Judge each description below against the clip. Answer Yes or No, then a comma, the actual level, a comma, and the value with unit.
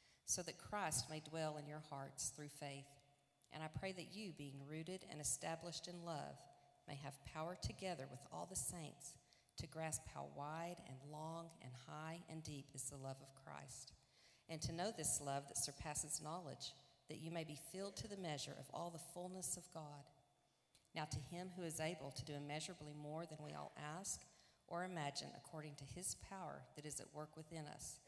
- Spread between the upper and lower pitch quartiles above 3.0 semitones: No, average, 2.7 semitones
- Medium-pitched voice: Yes, medium, 150 Hz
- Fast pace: No, average, 195 wpm